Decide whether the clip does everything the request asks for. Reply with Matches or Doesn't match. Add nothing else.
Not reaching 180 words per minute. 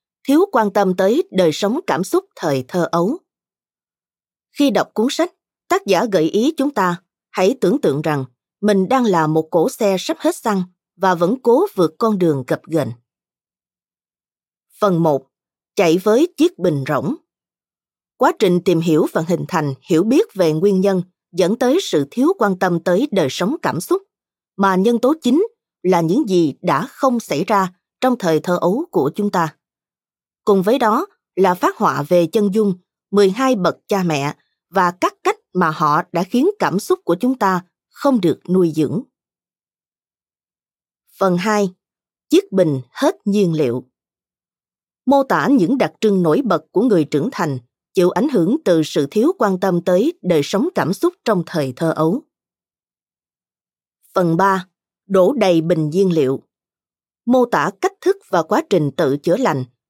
Matches